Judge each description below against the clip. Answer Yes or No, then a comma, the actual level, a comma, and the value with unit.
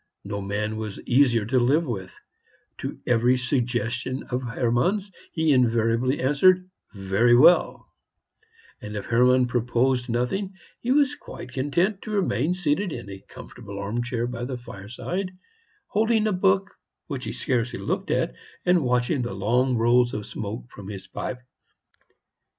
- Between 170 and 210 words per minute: No, average, 145 wpm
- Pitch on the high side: No, low, 125 Hz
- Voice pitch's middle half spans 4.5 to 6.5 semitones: Yes, average, 5.1 semitones